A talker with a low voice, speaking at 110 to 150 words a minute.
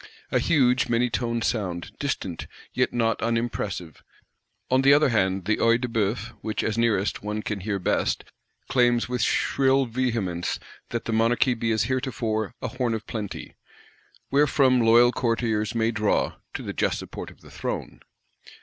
No: low, 115 Hz; average, 160 wpm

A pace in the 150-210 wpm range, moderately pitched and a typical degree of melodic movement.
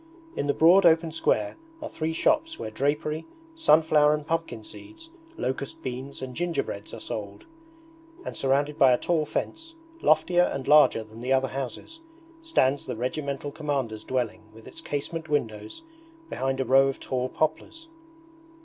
Yes: average, 155 wpm; medium, 145 Hz; average, 4.1 semitones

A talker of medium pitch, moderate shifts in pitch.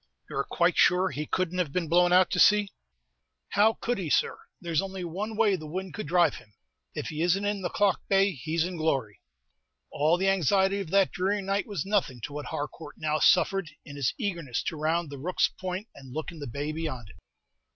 Yes: medium, 175 Hz; average, 4.2 semitones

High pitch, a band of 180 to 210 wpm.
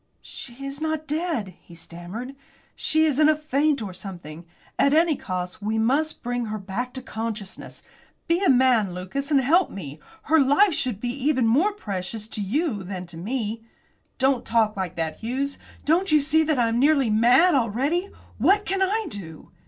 Yes: very high, 250 Hz; average, 185 wpm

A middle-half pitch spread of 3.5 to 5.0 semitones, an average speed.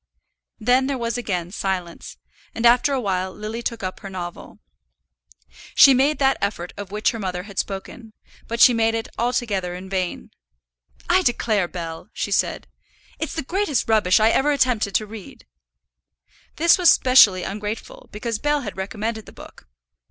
Yes: average, 4.7 semitones; average, 165 wpm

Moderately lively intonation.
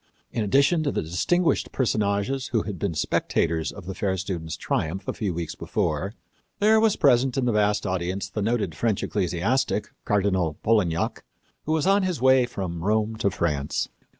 No: wide, 6.0 semitones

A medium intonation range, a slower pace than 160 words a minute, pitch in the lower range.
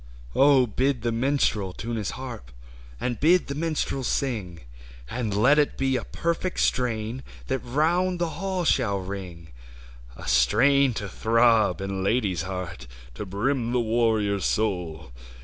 No: wide, 5.7 semitones; average, 140 wpm; low, 115 Hz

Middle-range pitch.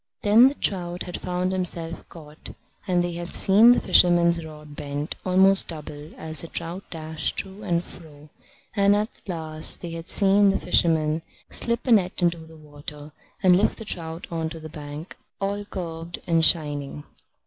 Yes: medium, 170 Hz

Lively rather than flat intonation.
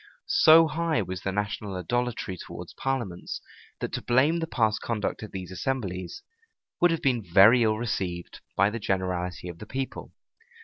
Yes: wide, 5.8 semitones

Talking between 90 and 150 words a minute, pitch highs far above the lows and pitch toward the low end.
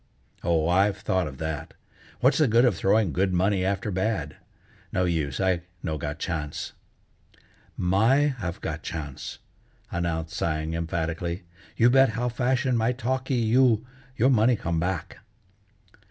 Yes: average, 140 wpm; wide, 6.1 semitones; very low, 95 Hz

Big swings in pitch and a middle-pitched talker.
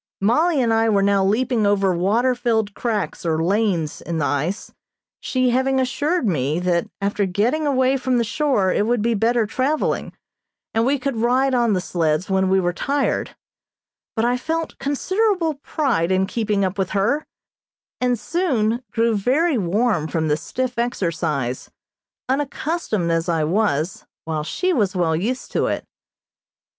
No: wide, 5.7 semitones; high, 220 Hz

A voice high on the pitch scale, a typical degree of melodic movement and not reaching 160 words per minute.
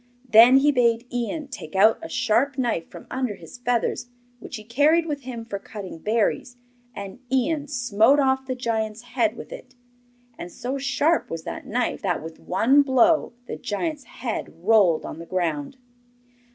No: high, 240 Hz; average, 4.1 semitones; average, 170 wpm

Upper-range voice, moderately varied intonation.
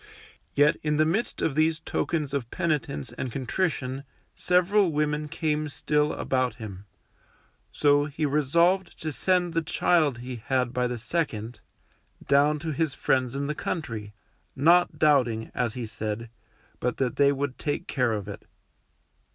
No: medium, 145 Hz; average, 4.0 semitones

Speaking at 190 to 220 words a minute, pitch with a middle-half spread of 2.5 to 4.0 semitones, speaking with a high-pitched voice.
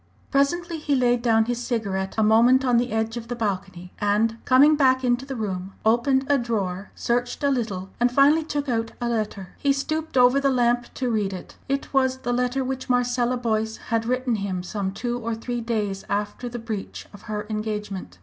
Yes: average, 200 wpm; average, 3.3 semitones; high, 240 Hz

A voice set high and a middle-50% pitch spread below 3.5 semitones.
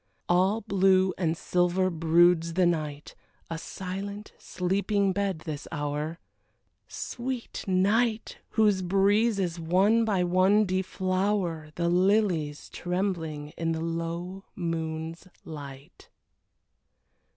No: medium, 180 Hz; average, 3.1 semitones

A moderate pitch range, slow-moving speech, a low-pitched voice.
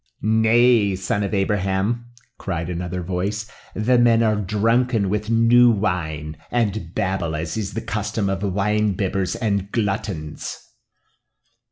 Yes: average, 3.0 semitones; slow, 130 wpm; low, 100 Hz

